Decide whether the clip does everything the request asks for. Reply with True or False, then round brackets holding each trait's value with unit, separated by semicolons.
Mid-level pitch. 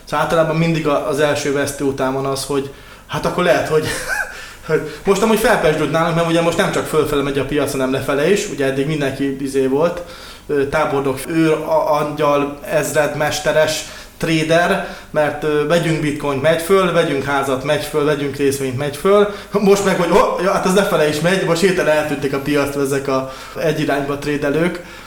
True (150 Hz)